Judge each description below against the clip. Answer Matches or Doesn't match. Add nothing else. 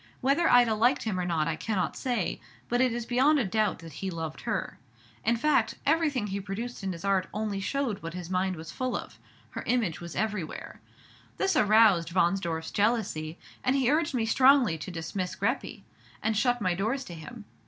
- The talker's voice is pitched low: Doesn't match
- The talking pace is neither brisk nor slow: Matches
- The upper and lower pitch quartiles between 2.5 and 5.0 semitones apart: Doesn't match